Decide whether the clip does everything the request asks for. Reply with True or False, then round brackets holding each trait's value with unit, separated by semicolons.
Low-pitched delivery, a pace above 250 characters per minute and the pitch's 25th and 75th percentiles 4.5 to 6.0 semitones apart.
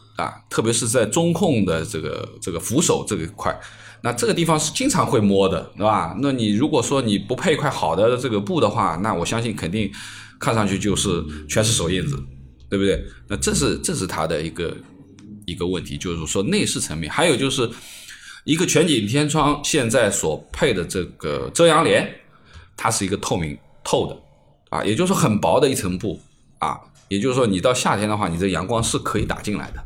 True (105 Hz; 295 characters per minute; 5.0 semitones)